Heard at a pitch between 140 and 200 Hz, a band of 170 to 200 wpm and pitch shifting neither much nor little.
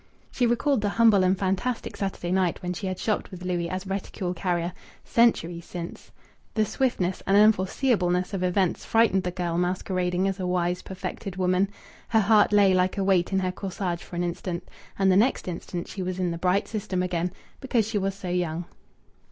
No: medium, 185 Hz; average, 195 wpm; narrow, 1.9 semitones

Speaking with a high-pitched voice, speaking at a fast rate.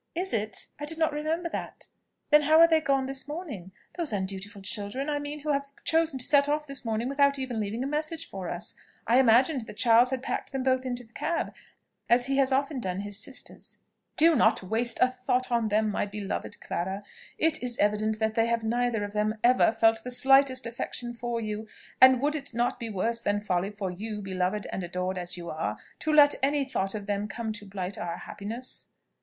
Yes: high, 240 Hz; fast, 215 wpm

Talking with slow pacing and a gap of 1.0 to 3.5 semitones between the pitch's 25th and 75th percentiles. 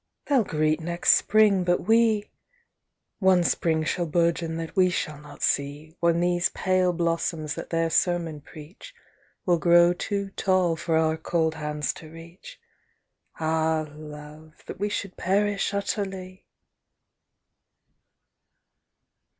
Yes: slow, 125 wpm; average, 2.9 semitones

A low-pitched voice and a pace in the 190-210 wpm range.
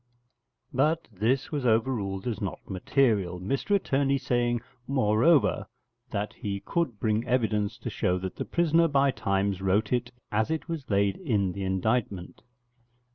No: low, 110 Hz; average, 145 wpm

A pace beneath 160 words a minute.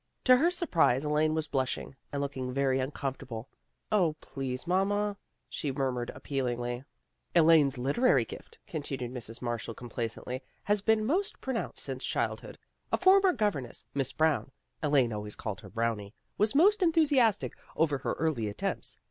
No: average, 165 wpm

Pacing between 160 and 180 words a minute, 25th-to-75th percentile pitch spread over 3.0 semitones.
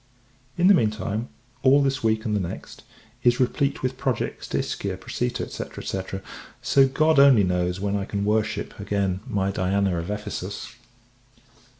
Yes: average, 165 wpm; average, 5.1 semitones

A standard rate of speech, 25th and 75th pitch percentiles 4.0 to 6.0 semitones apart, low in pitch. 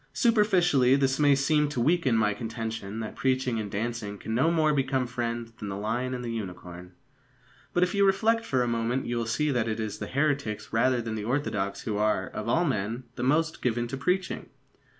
No: fast, 210 wpm; average, 4.6 semitones; low, 120 Hz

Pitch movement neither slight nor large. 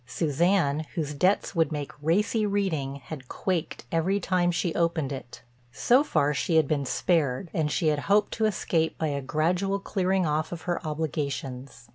Yes: average, 4.1 semitones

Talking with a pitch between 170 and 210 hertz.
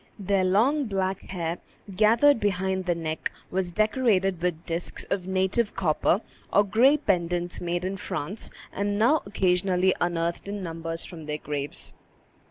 Yes: medium, 185 Hz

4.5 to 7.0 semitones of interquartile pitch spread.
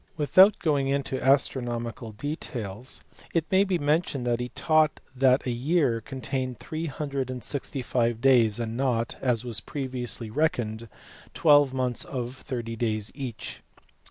No: average, 3.4 semitones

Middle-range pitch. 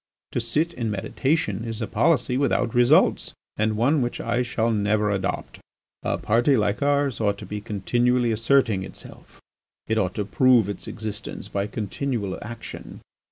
No: low, 115 Hz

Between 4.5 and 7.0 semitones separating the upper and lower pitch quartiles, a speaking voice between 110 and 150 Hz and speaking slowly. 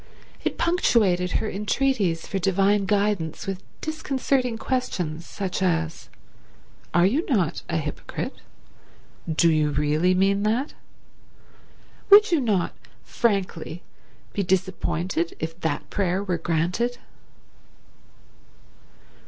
No: average, 4.9 semitones; high, 190 Hz; slow, 105 wpm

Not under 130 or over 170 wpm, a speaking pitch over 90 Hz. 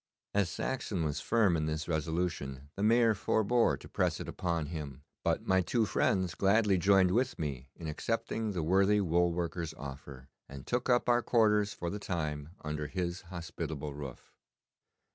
No: average, 165 wpm; very low, 85 Hz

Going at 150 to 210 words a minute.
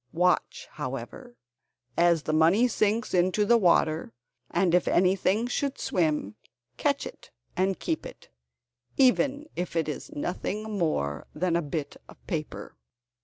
No: slow, 135 wpm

